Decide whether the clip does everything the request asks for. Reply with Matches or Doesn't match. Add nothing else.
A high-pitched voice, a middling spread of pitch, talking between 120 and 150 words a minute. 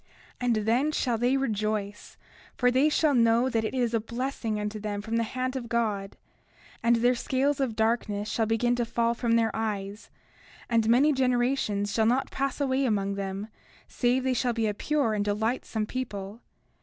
Doesn't match